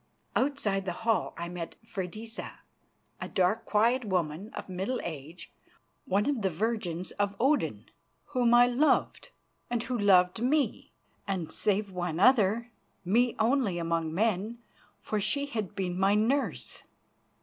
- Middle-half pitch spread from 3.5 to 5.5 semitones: Yes, average, 4.6 semitones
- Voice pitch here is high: Yes, high, 210 Hz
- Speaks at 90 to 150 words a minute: Yes, average, 140 wpm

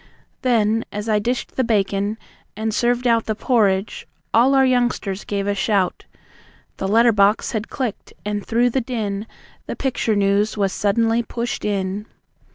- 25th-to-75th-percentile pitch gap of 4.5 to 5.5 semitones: No, average, 2.8 semitones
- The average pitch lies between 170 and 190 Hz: No, high, 220 Hz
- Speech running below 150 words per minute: No, average, 160 wpm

